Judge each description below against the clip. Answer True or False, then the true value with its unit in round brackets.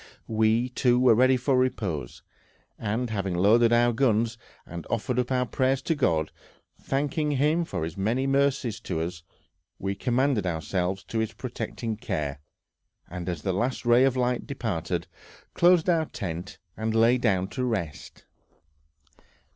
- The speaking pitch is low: True (115 Hz)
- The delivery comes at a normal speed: True (150 wpm)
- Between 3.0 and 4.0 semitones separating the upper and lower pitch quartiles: False (5.1 semitones)